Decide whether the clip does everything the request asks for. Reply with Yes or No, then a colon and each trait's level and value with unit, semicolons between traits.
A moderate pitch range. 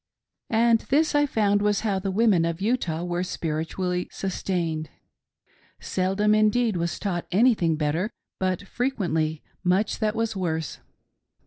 Yes: average, 4.1 semitones